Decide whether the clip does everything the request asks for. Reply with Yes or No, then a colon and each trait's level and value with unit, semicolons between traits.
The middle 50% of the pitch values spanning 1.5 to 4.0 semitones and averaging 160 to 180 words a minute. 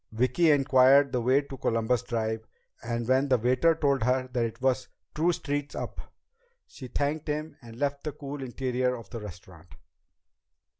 Yes: average, 3.3 semitones; average, 165 wpm